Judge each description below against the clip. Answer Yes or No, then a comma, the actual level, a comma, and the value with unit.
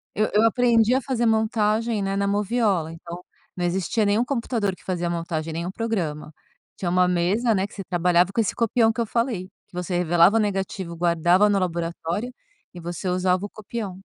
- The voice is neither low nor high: No, high, 195 Hz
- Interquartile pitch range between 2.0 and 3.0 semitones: No, average, 4.2 semitones